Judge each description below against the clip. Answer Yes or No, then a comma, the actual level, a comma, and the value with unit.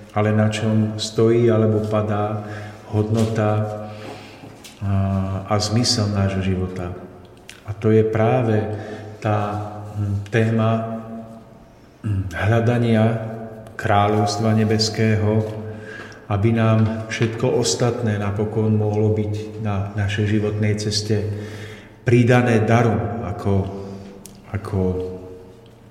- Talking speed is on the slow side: Yes, slow, 80 wpm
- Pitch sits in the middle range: No, low, 105 Hz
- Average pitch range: No, narrow, 1.2 semitones